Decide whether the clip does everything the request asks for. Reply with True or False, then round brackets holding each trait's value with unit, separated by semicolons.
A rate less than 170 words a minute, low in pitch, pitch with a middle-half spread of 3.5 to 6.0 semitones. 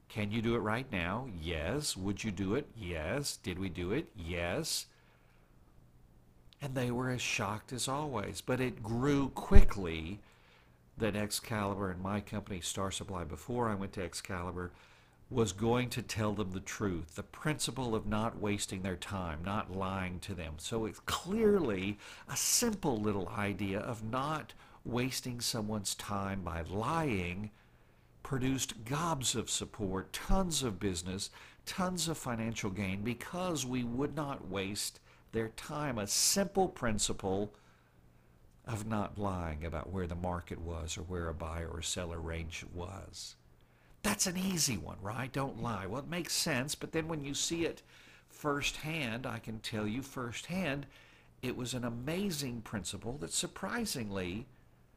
True (150 wpm; 105 Hz; 5.6 semitones)